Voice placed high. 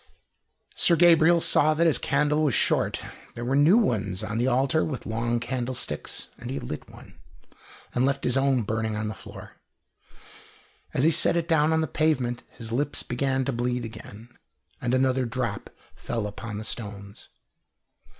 No: low, 125 Hz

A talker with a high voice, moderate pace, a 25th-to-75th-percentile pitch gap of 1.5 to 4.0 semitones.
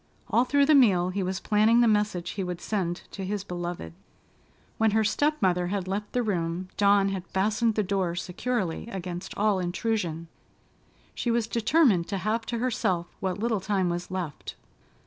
Yes: high, 195 Hz; average, 175 wpm; average, 3.7 semitones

